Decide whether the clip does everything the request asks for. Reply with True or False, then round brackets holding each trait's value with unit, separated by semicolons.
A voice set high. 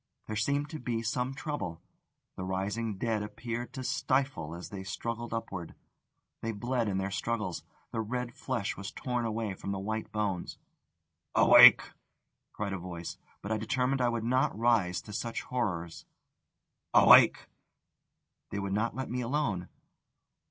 False (110 Hz)